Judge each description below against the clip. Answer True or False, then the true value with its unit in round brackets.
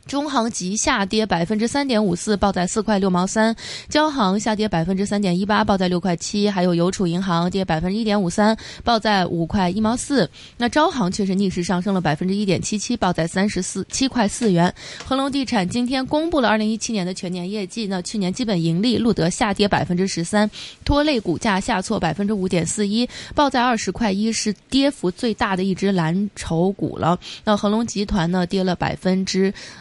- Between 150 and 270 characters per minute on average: False (320 characters per minute)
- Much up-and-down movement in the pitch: False (3.5 semitones)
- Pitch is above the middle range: True (205 Hz)